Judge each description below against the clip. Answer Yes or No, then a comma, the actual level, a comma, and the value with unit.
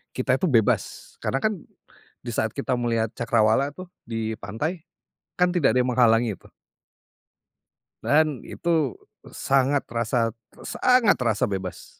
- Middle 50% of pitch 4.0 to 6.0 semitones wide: Yes, average, 5.0 semitones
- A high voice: No, low, 125 Hz